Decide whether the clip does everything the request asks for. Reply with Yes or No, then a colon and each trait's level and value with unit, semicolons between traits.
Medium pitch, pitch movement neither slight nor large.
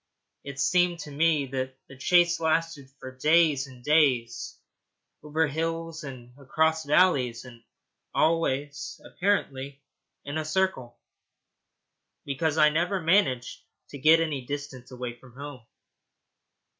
Yes: medium, 145 Hz; average, 3.8 semitones